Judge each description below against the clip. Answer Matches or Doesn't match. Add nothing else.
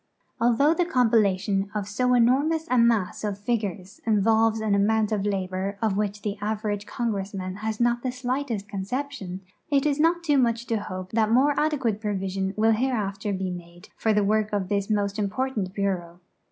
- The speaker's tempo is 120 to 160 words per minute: Doesn't match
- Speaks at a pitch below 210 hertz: Doesn't match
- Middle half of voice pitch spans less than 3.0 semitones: Doesn't match